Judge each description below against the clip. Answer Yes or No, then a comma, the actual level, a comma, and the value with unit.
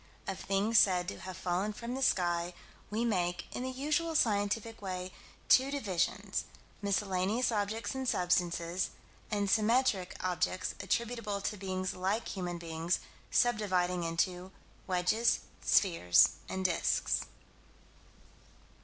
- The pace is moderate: No, slow, 120 wpm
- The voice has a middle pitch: No, high, 195 Hz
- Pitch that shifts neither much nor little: Yes, average, 3.7 semitones